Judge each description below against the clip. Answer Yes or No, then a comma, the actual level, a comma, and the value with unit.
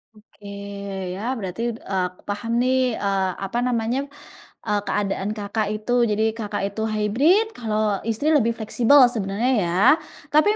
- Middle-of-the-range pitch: No, high, 215 Hz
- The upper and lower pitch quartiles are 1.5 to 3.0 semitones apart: Yes, average, 2.7 semitones